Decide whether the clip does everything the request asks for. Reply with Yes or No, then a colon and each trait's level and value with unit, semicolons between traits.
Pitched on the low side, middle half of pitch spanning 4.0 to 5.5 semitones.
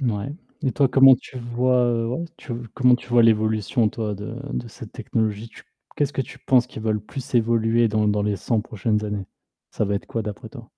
No: low, 115 Hz; average, 2.8 semitones